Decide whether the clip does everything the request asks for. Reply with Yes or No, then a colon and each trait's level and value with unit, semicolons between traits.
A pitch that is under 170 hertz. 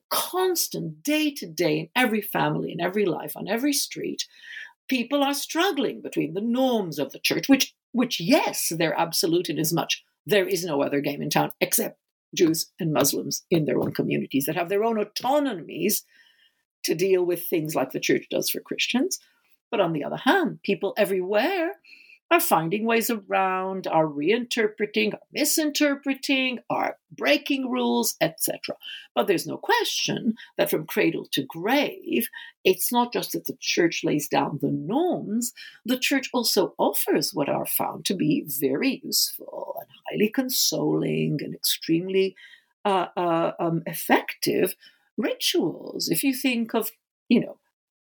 No: high, 240 Hz